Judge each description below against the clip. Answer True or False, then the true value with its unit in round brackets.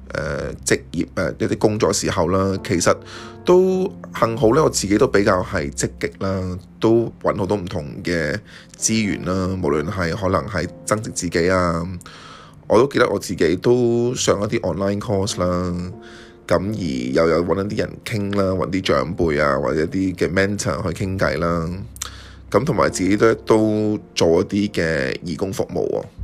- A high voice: False (95 Hz)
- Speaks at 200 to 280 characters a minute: True (270 characters per minute)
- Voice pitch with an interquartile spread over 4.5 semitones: False (3.2 semitones)